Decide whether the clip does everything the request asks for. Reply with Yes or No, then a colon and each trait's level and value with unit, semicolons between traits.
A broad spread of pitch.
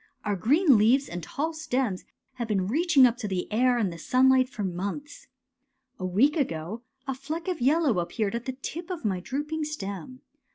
Yes: wide, 6.6 semitones